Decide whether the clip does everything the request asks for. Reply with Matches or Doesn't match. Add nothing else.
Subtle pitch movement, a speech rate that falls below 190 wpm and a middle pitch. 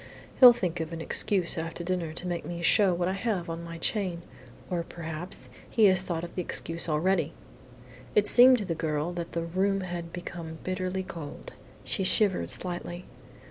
Matches